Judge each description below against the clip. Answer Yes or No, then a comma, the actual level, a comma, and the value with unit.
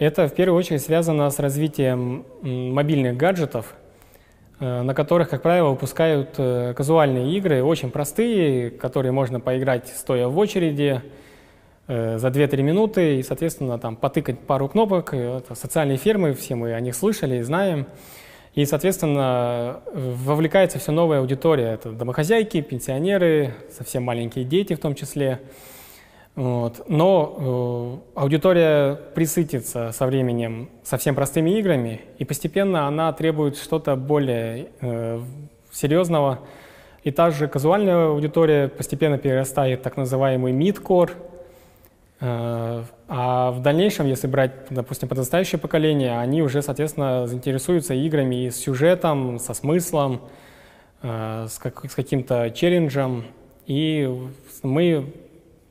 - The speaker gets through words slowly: No, average, 125 wpm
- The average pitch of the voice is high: No, medium, 140 Hz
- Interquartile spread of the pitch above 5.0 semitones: No, average, 3.9 semitones